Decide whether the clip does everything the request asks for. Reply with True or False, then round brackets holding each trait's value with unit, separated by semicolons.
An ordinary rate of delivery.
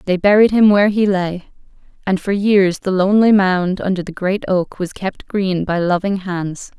True (195 wpm)